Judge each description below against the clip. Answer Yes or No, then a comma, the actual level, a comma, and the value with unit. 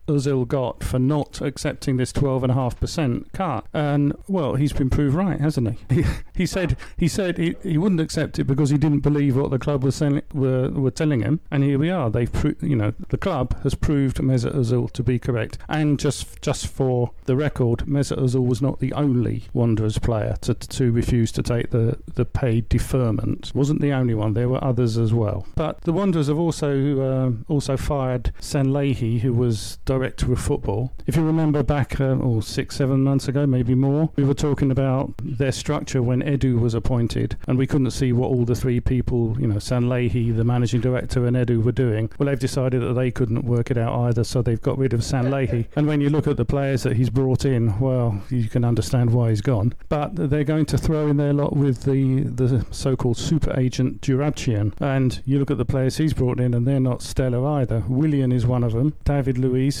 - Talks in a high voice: No, low, 130 Hz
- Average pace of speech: No, fast, 215 wpm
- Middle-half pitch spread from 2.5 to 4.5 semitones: Yes, average, 2.8 semitones